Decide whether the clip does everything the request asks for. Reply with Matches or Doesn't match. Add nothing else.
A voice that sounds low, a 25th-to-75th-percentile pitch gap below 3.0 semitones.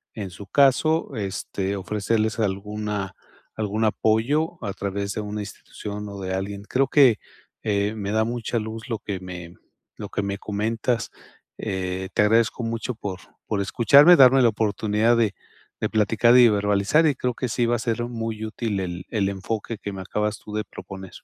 Matches